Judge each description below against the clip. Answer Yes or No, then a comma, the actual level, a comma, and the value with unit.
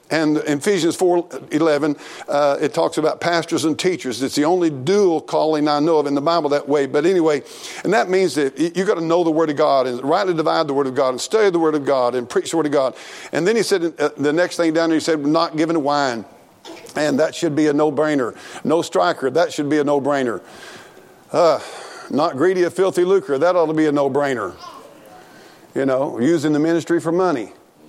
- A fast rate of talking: Yes, fast, 225 wpm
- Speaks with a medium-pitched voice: Yes, medium, 155 Hz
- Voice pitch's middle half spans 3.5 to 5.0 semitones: No, average, 2.9 semitones